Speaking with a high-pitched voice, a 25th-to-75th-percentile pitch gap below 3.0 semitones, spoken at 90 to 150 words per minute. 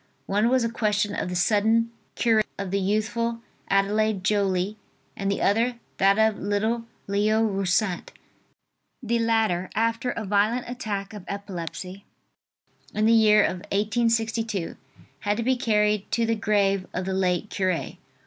Yes: high, 210 Hz; narrow, 2.4 semitones; average, 145 wpm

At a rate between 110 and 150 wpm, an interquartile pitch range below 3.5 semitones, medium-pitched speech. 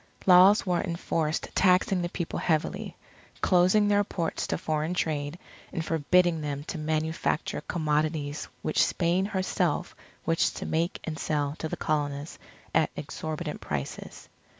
Yes: slow, 135 wpm; average, 2.8 semitones; medium, 160 Hz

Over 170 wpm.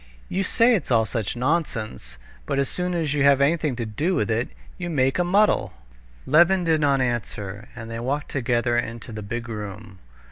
Yes: average, 190 wpm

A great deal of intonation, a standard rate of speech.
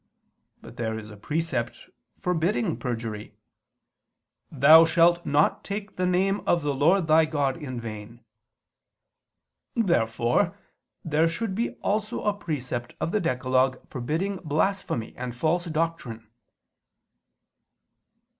No: wide, 6.5 semitones; slow, 115 wpm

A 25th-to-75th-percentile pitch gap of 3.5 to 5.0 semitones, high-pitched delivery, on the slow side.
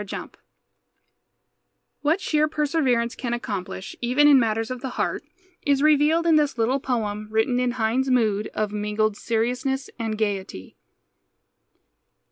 Yes: average, 4.4 semitones; high, 245 Hz; slow, 130 wpm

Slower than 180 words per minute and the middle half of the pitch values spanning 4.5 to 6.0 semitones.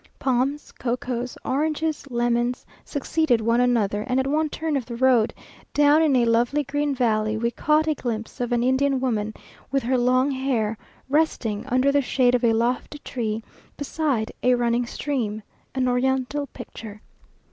No: average, 160 wpm; average, 3.1 semitones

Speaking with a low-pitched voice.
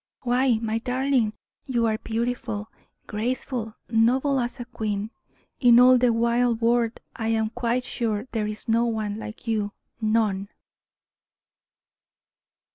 No: high, 230 Hz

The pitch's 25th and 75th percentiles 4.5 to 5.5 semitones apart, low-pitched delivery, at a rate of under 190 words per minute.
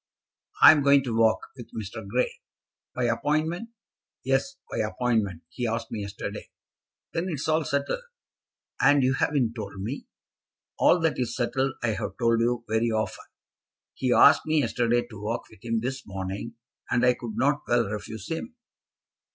No: average, 3.8 semitones; low, 120 Hz; average, 165 wpm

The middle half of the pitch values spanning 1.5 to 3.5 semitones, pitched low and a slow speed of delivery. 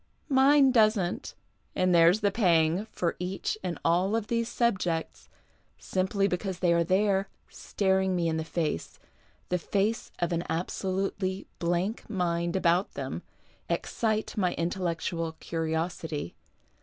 No: average, 3.0 semitones; medium, 185 Hz; slow, 130 wpm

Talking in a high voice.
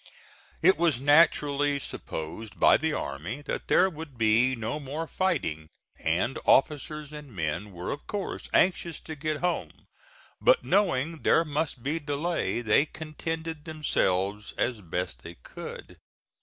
No: medium, 145 Hz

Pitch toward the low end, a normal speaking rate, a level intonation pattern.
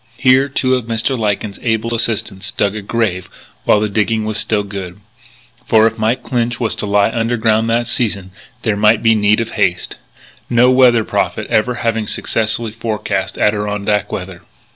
Yes: low, 110 Hz; average, 165 wpm; narrow, 2.1 semitones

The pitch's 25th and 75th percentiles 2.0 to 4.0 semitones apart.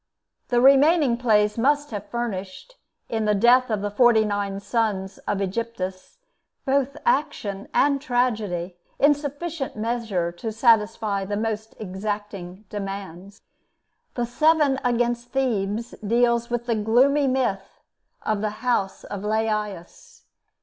Yes: average, 3.6 semitones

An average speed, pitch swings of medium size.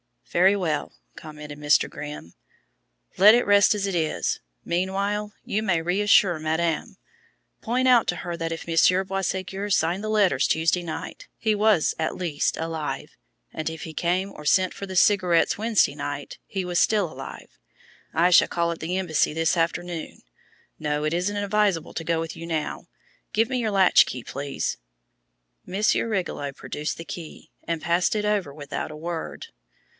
Yes: average, 170 wpm; average, 3.9 semitones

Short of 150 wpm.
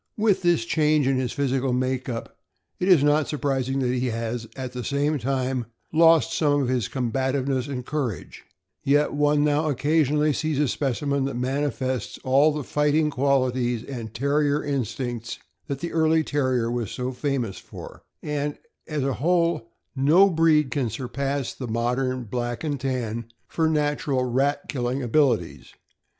No: average, 155 wpm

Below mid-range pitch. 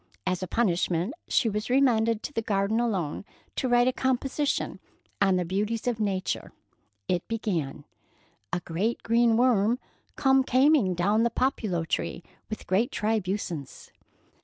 No: high, 220 Hz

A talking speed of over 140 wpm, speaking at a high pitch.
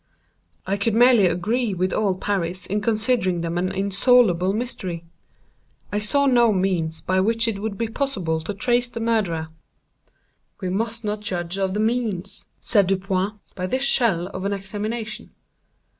Yes: average, 160 wpm; high, 200 Hz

